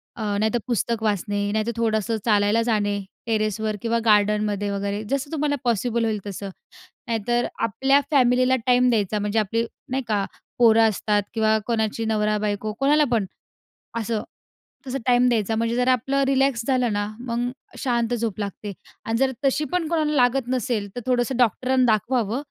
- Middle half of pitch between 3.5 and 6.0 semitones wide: No, average, 2.9 semitones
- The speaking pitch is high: Yes, high, 230 Hz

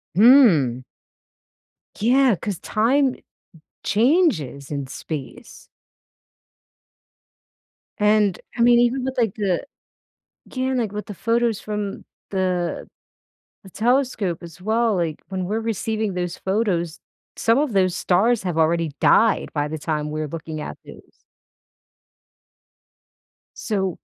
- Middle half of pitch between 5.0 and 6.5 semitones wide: Yes, wide, 5.6 semitones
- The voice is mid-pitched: No, high, 205 Hz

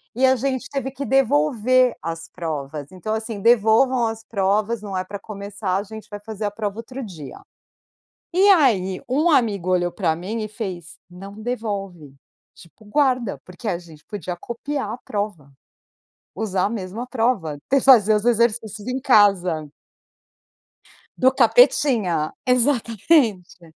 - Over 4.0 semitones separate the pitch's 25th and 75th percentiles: Yes, average, 4.9 semitones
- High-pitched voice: Yes, high, 215 Hz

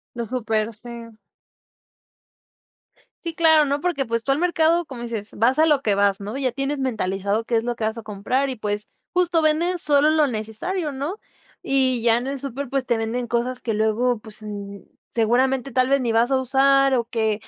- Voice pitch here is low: No, very high, 250 Hz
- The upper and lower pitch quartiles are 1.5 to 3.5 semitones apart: No, average, 3.9 semitones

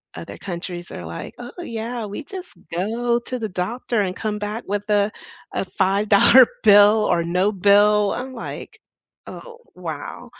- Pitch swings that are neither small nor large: Yes, average, 3.2 semitones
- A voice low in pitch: No, high, 210 Hz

